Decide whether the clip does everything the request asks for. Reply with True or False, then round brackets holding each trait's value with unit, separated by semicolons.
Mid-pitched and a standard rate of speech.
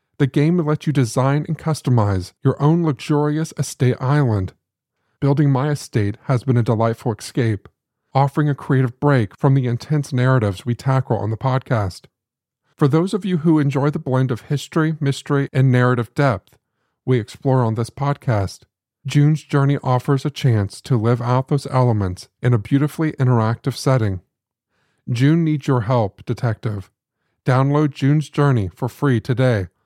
False (130 Hz; 160 wpm)